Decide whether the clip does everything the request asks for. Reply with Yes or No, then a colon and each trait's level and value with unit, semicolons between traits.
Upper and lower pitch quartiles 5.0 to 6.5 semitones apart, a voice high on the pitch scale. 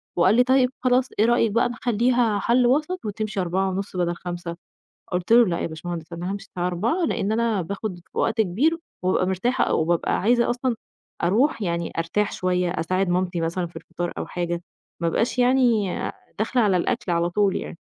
Yes: average, 5.3 semitones; high, 195 Hz